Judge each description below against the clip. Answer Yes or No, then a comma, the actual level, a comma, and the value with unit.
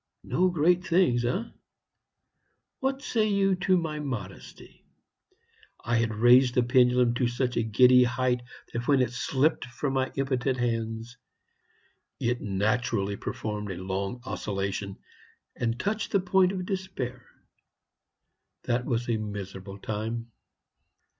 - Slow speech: Yes, slow, 125 wpm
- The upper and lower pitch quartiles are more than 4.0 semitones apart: Yes, average, 4.6 semitones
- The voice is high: No, low, 125 Hz